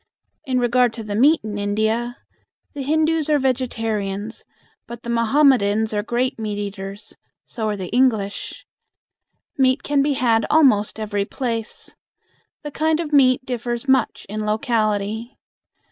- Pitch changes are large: No, average, 3.8 semitones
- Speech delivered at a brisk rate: No, average, 140 wpm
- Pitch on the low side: No, high, 235 Hz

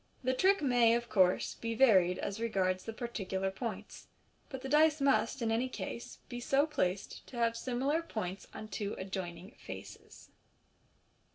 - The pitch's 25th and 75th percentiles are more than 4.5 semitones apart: Yes, average, 5.1 semitones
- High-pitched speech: Yes, high, 230 Hz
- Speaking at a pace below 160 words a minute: No, average, 165 wpm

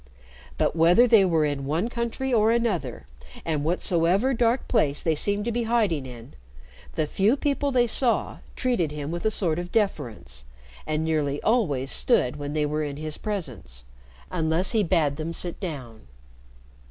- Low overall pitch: No, medium, 170 Hz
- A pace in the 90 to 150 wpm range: No, average, 165 wpm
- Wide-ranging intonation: Yes, wide, 7.1 semitones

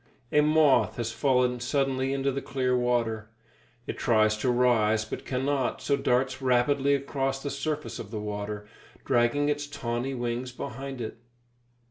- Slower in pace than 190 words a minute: Yes, average, 150 wpm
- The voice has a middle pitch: No, low, 130 Hz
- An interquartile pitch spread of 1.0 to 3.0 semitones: Yes, narrow, 2.6 semitones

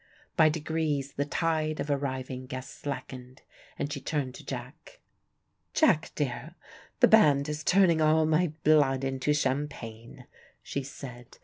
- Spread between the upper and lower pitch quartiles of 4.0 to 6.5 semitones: No, average, 2.8 semitones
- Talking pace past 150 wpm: No, slow, 135 wpm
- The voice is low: No, medium, 145 Hz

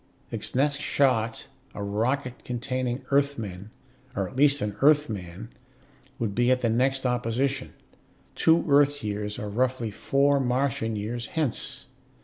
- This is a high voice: No, low, 125 Hz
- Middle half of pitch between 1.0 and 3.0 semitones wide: No, average, 4.0 semitones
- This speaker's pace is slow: Yes, slow, 130 wpm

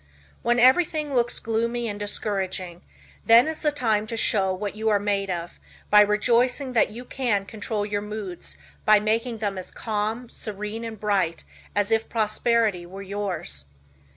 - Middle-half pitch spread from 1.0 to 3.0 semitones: Yes, average, 2.7 semitones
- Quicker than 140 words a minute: Yes, average, 160 wpm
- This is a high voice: Yes, high, 215 Hz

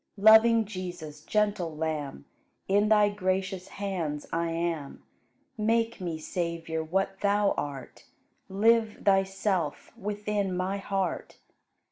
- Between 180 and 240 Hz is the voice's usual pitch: Yes, high, 190 Hz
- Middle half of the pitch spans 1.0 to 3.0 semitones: No, average, 3.8 semitones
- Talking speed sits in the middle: No, slow, 105 wpm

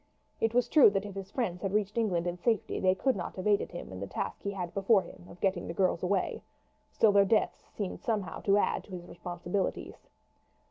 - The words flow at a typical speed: No, fast, 225 wpm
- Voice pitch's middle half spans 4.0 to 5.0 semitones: No, average, 2.8 semitones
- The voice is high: Yes, high, 195 Hz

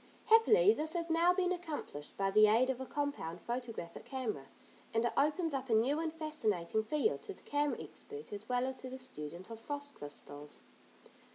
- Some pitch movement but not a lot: No, wide, 6.6 semitones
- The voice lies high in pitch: Yes, very high, 260 Hz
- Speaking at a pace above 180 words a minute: Yes, average, 190 wpm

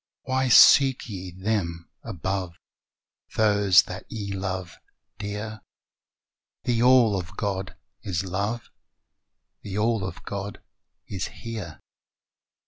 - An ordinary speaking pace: No, slow, 105 wpm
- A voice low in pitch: Yes, low, 100 Hz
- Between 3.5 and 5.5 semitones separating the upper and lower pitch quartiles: No, average, 2.9 semitones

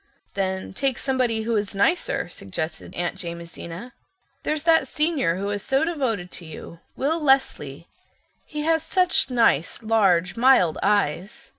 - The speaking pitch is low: No, high, 220 Hz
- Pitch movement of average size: No, wide, 7.6 semitones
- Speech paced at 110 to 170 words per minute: Yes, slow, 135 wpm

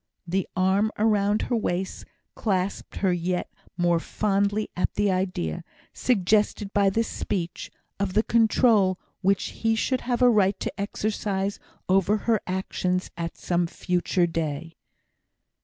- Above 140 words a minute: No, slow, 135 wpm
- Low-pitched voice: No, high, 195 Hz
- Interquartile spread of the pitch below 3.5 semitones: Yes, average, 2.7 semitones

